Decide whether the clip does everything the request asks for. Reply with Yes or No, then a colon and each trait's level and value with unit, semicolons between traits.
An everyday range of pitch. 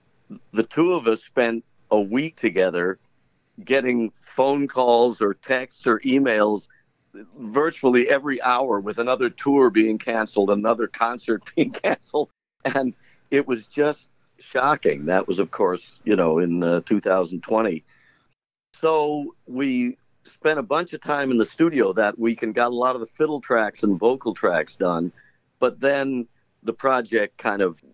Yes: average, 3.8 semitones